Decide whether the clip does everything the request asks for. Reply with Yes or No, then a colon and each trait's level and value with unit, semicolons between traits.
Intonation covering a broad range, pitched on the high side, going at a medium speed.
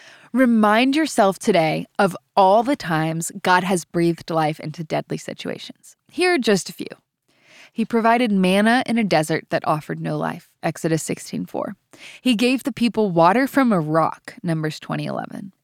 Yes: wide, 6.1 semitones; high, 200 Hz; average, 165 wpm